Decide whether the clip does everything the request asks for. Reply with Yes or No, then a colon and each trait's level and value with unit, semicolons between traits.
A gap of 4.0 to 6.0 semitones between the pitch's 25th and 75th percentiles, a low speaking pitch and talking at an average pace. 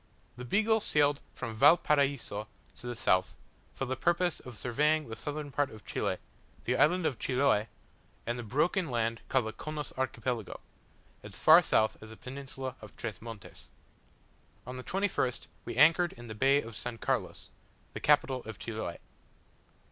Yes: average, 4.4 semitones; low, 130 Hz; average, 165 wpm